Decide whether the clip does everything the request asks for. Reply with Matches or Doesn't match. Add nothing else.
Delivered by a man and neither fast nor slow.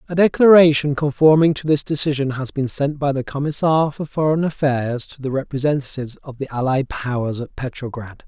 Matches